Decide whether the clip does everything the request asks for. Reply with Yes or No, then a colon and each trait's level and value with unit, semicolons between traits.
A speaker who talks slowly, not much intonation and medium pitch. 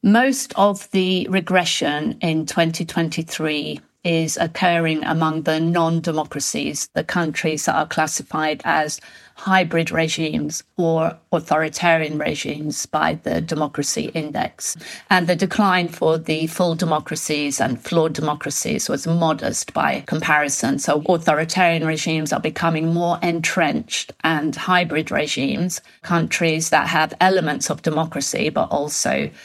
Yes: slow, 120 wpm; narrow, 2.1 semitones; medium, 165 Hz